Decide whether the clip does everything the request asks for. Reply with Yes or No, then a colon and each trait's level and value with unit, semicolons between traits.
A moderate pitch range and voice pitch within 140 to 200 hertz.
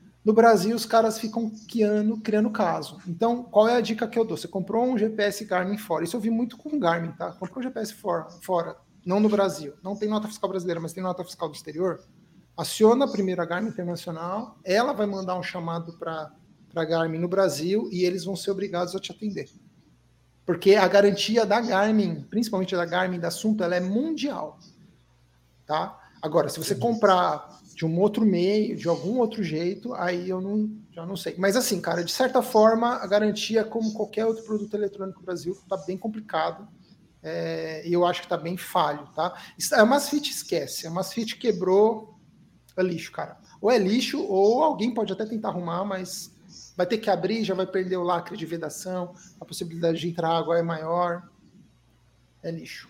Yes: average, 3.8 semitones; high, 190 Hz